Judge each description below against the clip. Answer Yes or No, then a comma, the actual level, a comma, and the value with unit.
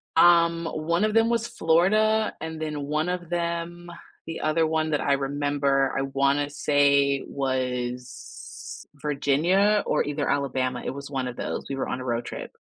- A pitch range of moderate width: Yes, average, 3.6 semitones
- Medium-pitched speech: Yes, medium, 145 Hz